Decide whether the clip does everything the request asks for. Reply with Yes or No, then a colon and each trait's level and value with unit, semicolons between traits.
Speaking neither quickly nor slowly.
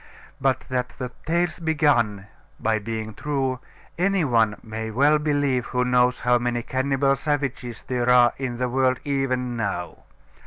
Yes: average, 150 wpm